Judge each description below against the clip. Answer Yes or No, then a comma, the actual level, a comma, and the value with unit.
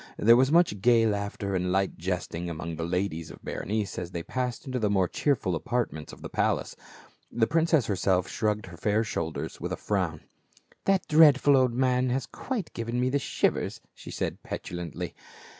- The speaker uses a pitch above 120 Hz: No, low, 110 Hz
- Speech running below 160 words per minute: No, average, 185 wpm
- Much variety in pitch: Yes, wide, 5.9 semitones